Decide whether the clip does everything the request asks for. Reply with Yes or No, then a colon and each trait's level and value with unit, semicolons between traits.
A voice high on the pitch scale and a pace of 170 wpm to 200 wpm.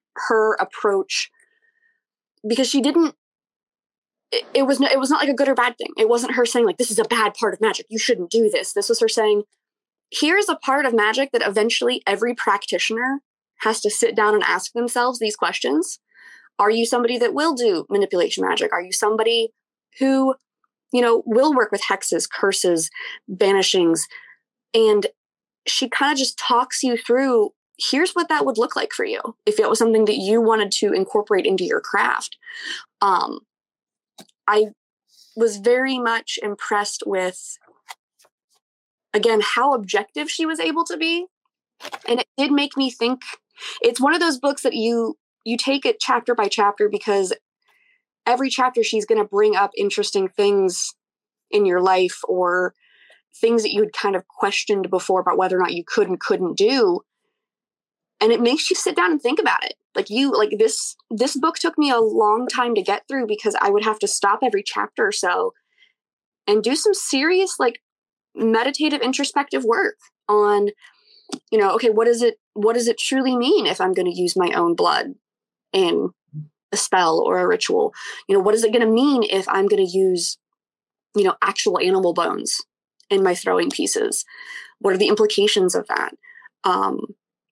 Yes: very high, 255 Hz; average, 185 wpm